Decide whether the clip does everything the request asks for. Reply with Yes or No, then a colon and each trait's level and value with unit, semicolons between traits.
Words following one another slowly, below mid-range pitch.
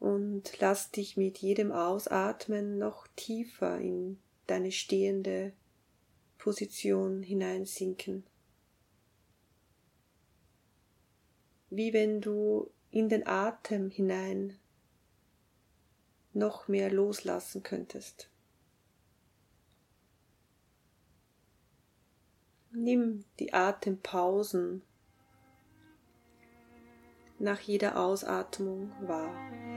No: slow, 60 wpm; high, 195 Hz